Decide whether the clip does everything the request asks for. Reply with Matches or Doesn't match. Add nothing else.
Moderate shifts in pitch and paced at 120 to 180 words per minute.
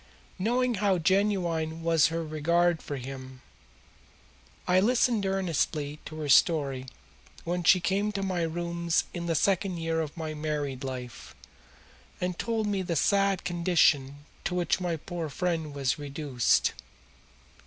Matches